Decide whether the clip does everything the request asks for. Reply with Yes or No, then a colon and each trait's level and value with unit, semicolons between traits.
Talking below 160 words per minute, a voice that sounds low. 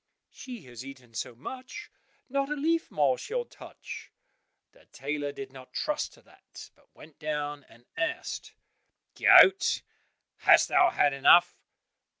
No: average, 140 wpm; medium, 150 Hz